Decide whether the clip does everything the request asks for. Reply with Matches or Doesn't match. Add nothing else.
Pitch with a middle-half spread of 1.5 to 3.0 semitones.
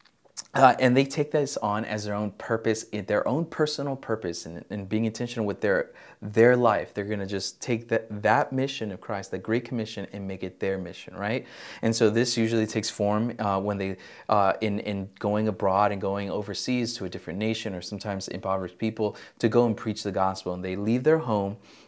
Matches